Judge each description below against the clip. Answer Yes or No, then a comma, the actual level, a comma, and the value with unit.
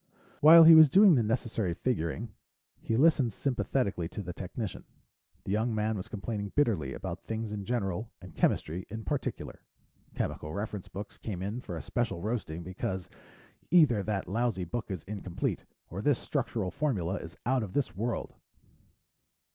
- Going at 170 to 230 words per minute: No, average, 160 wpm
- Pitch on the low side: Yes, low, 110 Hz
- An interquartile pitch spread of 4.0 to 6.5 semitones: Yes, average, 4.5 semitones